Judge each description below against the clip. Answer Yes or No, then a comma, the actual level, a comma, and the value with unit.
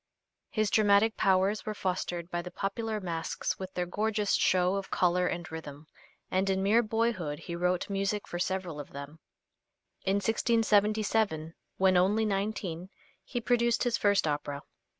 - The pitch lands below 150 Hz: No, high, 190 Hz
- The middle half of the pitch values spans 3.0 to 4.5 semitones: Yes, average, 3.4 semitones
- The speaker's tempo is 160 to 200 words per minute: No, average, 150 wpm